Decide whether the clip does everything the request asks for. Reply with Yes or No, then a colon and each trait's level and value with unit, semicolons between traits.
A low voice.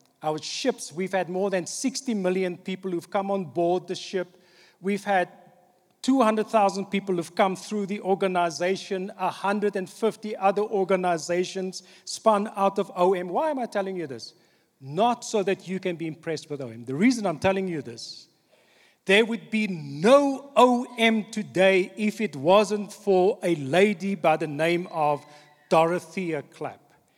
No: high, 190 Hz